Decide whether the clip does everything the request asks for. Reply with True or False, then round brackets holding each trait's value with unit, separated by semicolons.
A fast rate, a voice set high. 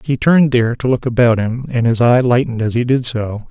False (255 wpm; 120 Hz)